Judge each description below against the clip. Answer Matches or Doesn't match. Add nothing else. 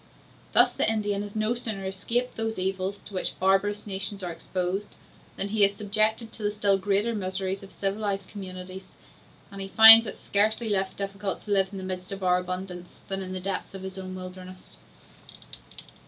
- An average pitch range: Doesn't match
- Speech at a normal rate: Matches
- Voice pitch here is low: Doesn't match